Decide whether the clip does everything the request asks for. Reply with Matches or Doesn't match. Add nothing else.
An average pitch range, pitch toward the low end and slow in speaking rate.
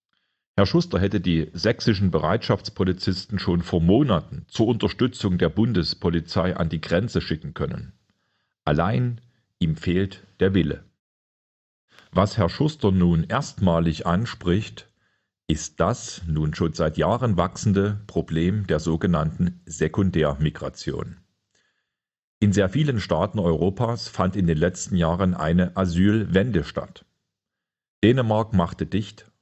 Matches